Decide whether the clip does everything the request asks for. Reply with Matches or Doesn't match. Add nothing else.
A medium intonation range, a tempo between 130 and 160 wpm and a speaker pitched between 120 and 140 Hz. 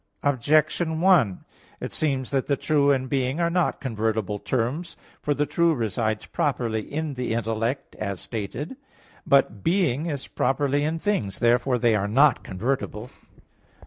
Matches